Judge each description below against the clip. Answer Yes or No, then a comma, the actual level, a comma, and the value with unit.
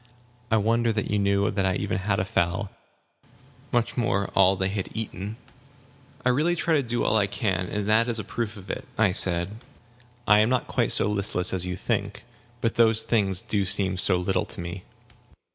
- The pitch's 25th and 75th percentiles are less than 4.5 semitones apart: Yes, average, 2.8 semitones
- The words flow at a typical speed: No, fast, 210 wpm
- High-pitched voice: No, low, 100 Hz